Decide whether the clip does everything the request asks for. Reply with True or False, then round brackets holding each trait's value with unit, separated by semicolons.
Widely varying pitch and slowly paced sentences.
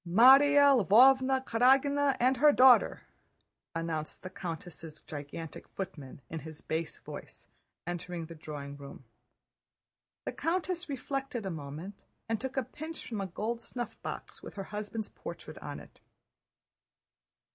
True (8.3 semitones; 130 wpm)